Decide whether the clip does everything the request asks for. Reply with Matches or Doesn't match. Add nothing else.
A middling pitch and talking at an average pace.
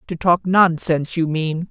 Matches